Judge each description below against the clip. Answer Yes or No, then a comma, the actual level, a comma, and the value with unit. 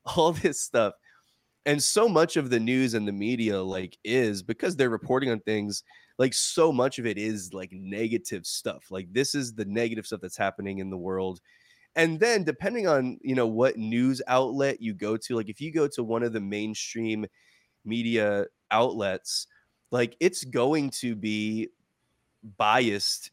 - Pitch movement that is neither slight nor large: Yes, average, 3.6 semitones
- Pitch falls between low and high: No, low, 115 Hz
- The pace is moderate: Yes, average, 175 wpm